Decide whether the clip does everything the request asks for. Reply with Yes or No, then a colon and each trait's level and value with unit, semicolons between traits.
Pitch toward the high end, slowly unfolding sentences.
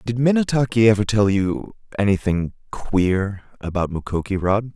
No: low, 105 Hz; slow, 90 wpm